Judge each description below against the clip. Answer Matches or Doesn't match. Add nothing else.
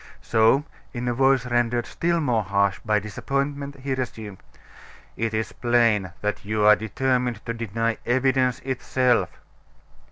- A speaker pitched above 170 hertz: Doesn't match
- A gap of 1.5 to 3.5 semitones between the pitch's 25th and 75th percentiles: Matches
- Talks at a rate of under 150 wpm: Matches